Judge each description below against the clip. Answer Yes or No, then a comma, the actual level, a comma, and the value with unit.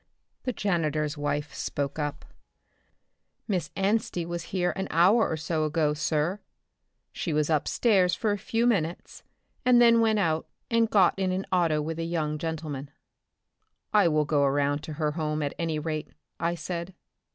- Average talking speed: Yes, average, 165 wpm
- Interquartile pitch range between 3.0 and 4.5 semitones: Yes, average, 3.9 semitones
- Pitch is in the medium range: Yes, medium, 165 Hz